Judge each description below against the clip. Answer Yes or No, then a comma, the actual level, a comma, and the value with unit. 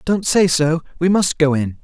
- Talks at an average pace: No, fast, 230 wpm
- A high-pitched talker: No, medium, 165 Hz